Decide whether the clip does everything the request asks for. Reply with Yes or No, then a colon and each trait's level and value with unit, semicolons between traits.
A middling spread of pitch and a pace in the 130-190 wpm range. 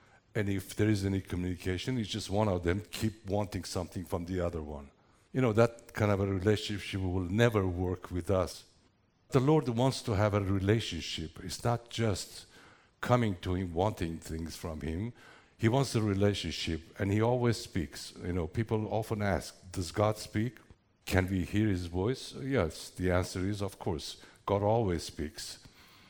Yes: average, 3.4 semitones; average, 175 wpm